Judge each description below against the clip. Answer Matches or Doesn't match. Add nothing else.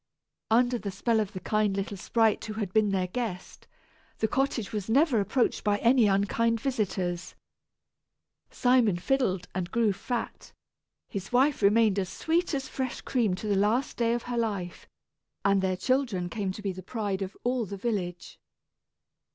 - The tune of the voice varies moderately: Matches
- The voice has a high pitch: Matches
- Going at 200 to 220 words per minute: Doesn't match